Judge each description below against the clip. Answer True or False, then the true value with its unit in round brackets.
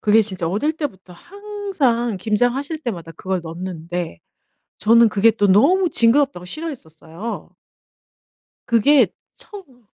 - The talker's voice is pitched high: True (230 Hz)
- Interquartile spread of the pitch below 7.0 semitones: False (7.6 semitones)